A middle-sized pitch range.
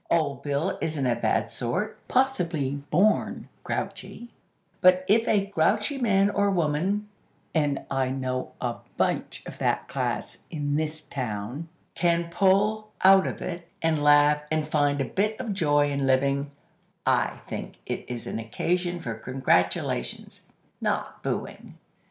No: wide, 5.7 semitones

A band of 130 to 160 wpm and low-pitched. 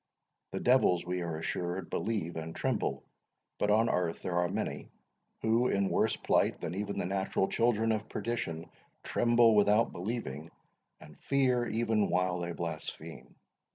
Yes: average, 150 wpm; very low, 95 Hz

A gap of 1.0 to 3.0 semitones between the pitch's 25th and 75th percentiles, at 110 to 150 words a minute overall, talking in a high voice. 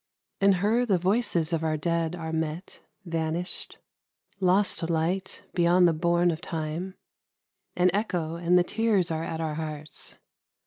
No: narrow, 2.4 semitones; average, 145 wpm; medium, 170 Hz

